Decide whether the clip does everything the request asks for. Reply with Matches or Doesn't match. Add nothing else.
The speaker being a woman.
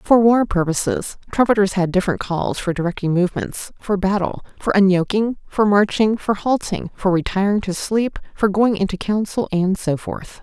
Matches